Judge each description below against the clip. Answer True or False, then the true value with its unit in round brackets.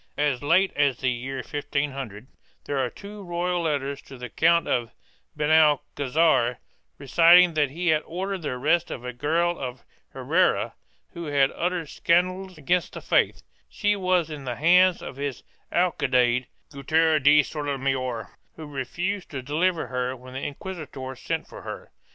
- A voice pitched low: False (150 Hz)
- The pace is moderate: True (155 wpm)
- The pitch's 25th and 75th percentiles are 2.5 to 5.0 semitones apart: True (4.6 semitones)